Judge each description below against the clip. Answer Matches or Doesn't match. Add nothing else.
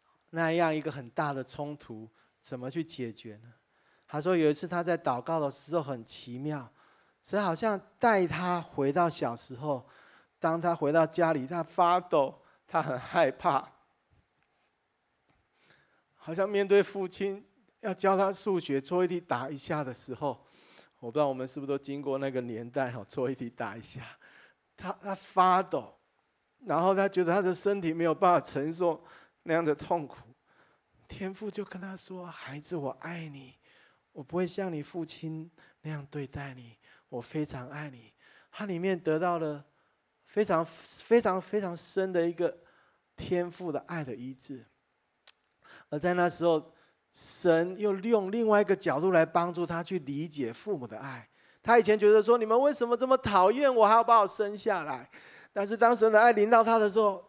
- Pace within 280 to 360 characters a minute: Doesn't match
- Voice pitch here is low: Doesn't match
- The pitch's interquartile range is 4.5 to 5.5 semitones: Matches